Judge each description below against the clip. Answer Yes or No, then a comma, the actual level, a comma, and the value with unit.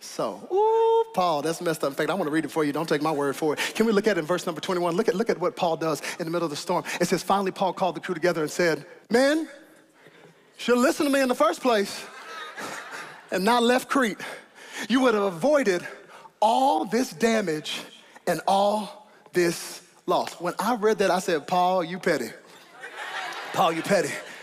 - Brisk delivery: Yes, fast, 220 wpm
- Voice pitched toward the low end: No, high, 190 Hz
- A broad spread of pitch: Yes, wide, 5.7 semitones